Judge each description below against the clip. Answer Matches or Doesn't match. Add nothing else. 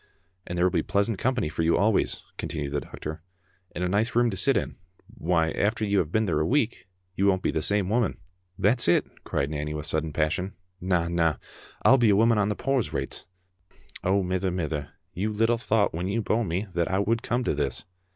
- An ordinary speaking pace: Doesn't match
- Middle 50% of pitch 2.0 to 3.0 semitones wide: Doesn't match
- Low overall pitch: Matches